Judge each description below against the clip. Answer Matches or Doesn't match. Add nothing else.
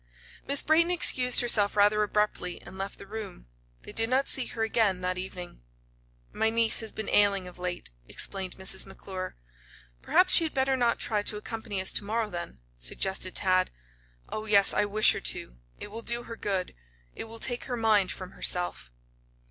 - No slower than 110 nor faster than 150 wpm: Doesn't match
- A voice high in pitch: Matches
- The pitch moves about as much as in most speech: Matches